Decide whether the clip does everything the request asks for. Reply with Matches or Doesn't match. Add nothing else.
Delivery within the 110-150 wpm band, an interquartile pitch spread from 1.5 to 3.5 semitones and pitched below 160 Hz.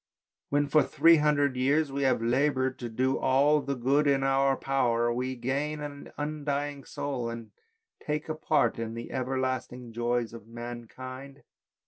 Doesn't match